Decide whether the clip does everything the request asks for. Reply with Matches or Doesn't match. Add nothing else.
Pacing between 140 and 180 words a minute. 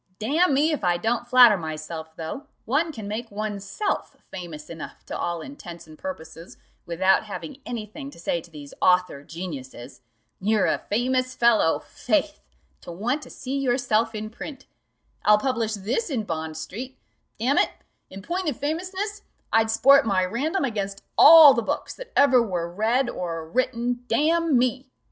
Matches